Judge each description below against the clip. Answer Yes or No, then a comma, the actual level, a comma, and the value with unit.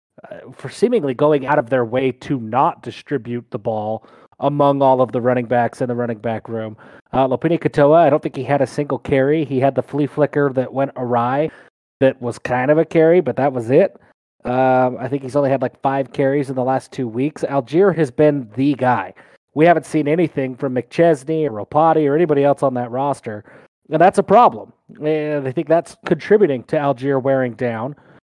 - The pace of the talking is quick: Yes, fast, 210 wpm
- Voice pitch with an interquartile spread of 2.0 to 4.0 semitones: Yes, average, 2.8 semitones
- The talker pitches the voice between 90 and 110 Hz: No, low, 135 Hz